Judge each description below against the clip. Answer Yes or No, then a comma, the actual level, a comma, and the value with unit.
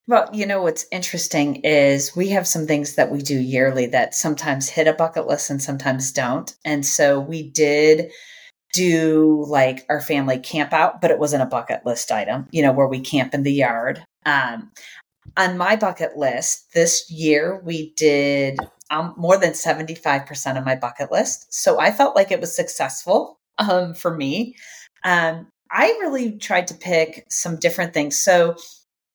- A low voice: No, medium, 155 Hz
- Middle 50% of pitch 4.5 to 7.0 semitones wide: No, average, 3.8 semitones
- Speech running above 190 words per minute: No, average, 180 wpm